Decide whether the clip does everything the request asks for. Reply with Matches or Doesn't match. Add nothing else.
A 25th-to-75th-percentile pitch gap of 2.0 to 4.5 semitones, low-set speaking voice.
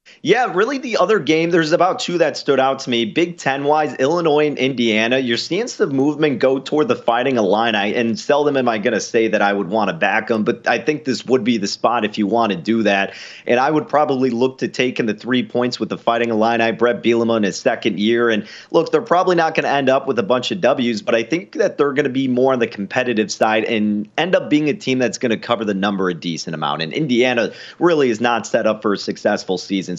Doesn't match